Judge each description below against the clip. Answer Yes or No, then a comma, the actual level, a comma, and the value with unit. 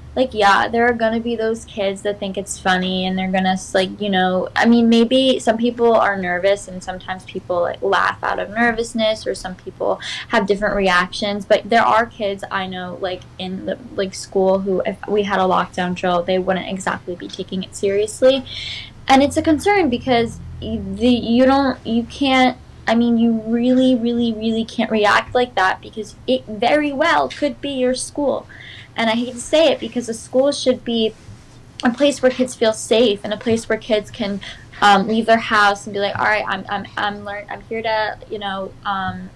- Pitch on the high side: Yes, high, 220 Hz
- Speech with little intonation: No, average, 3.9 semitones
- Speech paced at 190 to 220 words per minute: Yes, fast, 205 wpm